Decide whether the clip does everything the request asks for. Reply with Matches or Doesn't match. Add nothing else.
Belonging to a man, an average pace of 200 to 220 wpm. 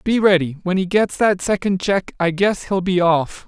Matches